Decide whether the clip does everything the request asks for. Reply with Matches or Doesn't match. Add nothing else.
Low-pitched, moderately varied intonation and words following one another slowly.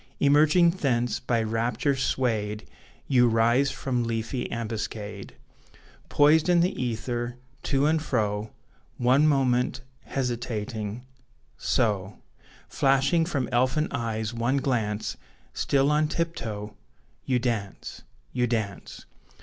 Matches